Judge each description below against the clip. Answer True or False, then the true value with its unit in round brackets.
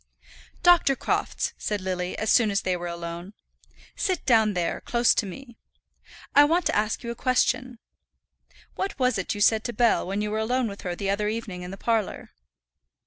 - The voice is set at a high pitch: True (215 Hz)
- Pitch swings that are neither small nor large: True (4.2 semitones)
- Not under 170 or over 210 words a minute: True (195 wpm)